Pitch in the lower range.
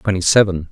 Yes: very low, 95 Hz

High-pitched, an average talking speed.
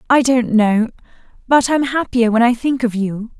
Yes: high, 240 Hz; average, 175 wpm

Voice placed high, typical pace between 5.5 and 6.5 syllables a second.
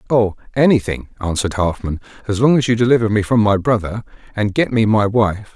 No: low, 110 Hz; 5.8 syllables/s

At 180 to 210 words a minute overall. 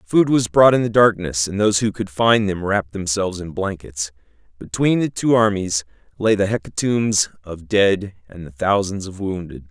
Yes: average, 185 wpm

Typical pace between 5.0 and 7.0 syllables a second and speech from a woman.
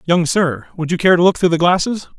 No: 5.9 syllables/s; male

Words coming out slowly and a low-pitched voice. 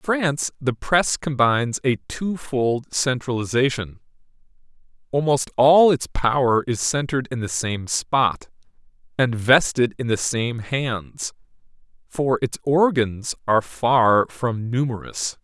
Yes: slow, 120 wpm; low, 130 Hz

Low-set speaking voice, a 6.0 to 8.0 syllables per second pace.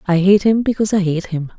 No: high, 190 Hz; 6.3 syllables/s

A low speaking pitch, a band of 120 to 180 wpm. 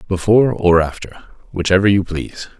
Yes: very low, 95 Hz; average, 140 wpm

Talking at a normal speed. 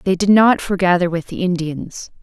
Yes: average, 190 wpm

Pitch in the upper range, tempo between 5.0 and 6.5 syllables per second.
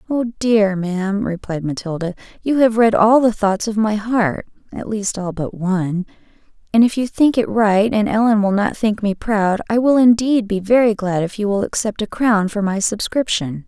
No: high, 210 Hz; 4.5 syllables/s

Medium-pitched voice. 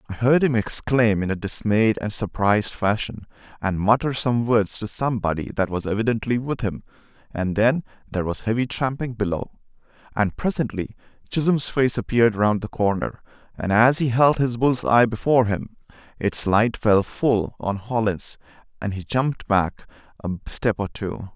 No: low, 110 Hz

